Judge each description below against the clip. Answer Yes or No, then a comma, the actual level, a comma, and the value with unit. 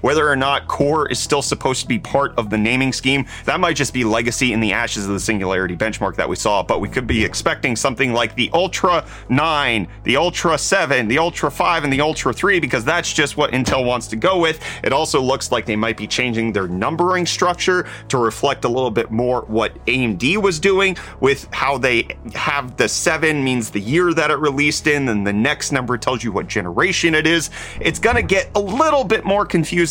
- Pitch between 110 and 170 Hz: Yes, low, 135 Hz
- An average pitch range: No, wide, 6.0 semitones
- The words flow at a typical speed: No, fast, 220 wpm